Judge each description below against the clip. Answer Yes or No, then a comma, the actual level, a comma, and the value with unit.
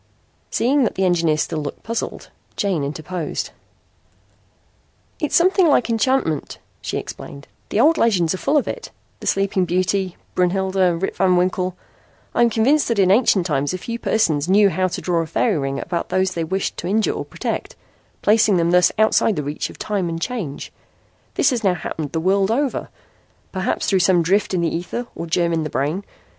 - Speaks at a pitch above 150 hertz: Yes, medium, 185 Hz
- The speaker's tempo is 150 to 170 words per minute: No, average, 190 wpm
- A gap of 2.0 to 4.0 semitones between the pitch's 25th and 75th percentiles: No, average, 4.5 semitones